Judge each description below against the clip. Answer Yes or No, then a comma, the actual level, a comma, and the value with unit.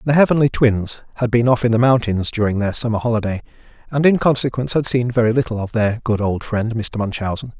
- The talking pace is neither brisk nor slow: No, fast, 215 wpm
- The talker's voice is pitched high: No, low, 115 Hz